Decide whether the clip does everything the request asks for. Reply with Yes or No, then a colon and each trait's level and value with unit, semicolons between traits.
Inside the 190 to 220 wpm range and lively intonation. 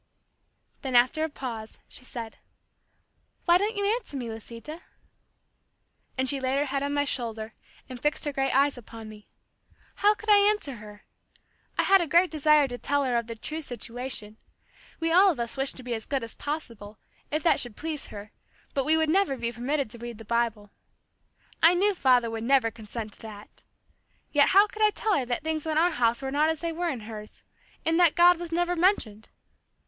Yes: fast, 205 wpm; wide, 5.8 semitones